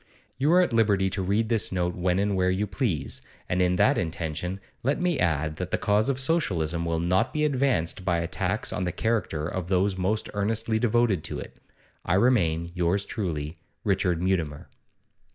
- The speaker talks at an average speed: Yes, average, 185 wpm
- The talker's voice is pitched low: Yes, very low, 95 Hz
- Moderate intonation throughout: Yes, average, 4.2 semitones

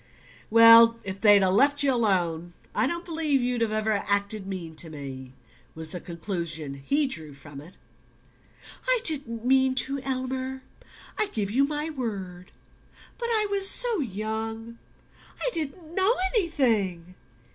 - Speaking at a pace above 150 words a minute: No, average, 145 wpm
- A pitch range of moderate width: No, wide, 7.2 semitones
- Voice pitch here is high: Yes, high, 230 Hz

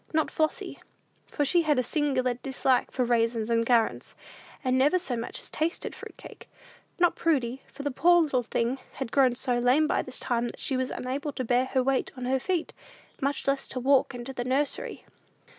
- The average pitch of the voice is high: Yes, very high, 260 Hz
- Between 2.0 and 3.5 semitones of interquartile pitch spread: Yes, average, 2.7 semitones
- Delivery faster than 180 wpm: Yes, average, 200 wpm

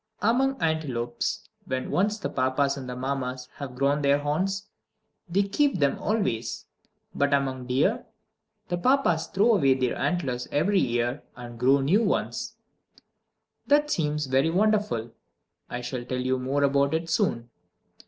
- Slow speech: No, average, 150 wpm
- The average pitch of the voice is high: No, medium, 140 Hz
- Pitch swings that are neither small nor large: No, wide, 6.6 semitones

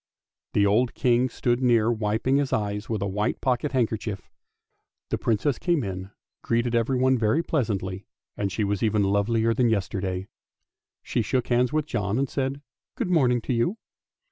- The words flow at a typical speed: Yes, average, 170 wpm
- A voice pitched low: Yes, low, 115 Hz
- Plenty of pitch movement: No, average, 3.9 semitones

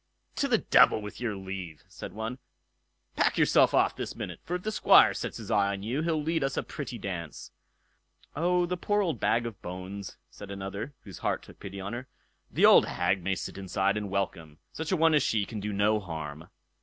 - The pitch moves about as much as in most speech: No, wide, 7.2 semitones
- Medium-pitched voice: No, low, 105 Hz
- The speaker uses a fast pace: Yes, fast, 215 wpm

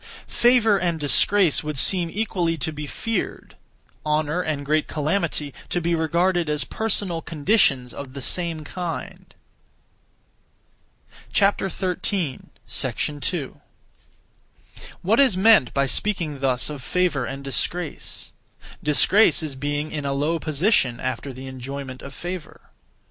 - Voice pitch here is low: No, medium, 155 Hz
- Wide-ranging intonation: No, average, 4.5 semitones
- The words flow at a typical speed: No, slow, 120 wpm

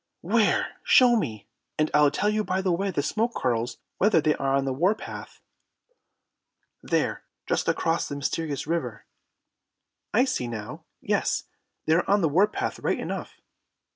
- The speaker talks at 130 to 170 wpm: Yes, average, 160 wpm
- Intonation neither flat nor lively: No, wide, 7.0 semitones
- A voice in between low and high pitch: Yes, medium, 165 Hz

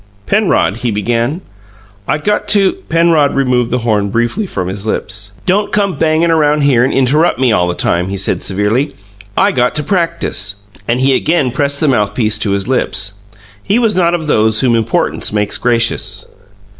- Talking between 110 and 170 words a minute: No, average, 180 wpm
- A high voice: No, low, 125 Hz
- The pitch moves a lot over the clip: Yes, wide, 7.0 semitones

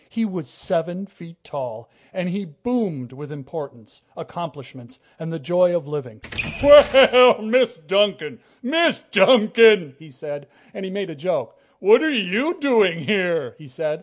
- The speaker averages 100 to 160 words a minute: Yes, average, 150 wpm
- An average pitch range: No, wide, 6.7 semitones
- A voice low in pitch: No, medium, 175 Hz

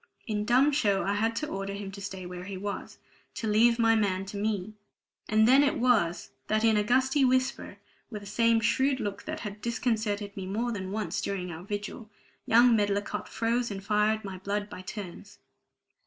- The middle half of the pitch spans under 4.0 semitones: Yes, average, 2.7 semitones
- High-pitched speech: Yes, high, 210 Hz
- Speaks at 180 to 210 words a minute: Yes, average, 195 wpm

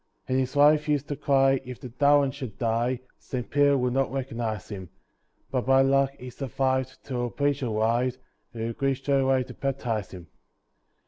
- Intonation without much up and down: Yes, narrow, 2.2 semitones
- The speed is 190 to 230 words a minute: No, average, 175 wpm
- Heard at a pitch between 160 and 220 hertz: No, low, 130 Hz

